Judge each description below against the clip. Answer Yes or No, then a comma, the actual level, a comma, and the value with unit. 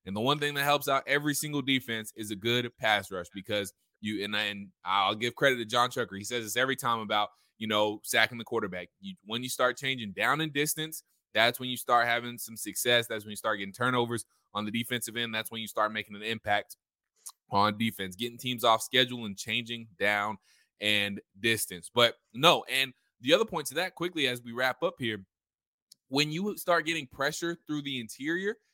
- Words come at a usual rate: No, fast, 215 wpm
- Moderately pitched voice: No, low, 120 Hz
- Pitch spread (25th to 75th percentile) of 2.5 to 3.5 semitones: No, average, 4.2 semitones